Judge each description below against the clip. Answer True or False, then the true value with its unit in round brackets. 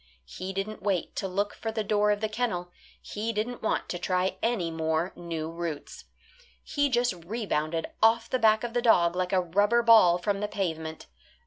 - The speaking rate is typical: True (190 wpm)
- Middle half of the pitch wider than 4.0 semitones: True (4.4 semitones)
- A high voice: True (195 Hz)